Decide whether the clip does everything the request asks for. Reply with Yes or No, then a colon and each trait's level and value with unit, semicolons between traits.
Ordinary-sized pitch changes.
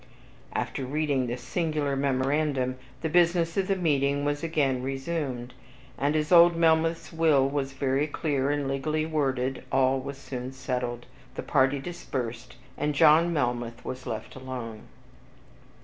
Yes: average, 3.2 semitones